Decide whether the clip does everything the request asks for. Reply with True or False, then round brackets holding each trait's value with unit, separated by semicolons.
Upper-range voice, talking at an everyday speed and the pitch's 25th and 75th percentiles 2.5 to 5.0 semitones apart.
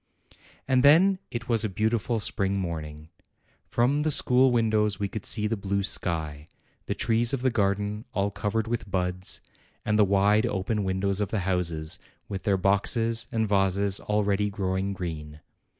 False (100 Hz; 165 wpm; 3.0 semitones)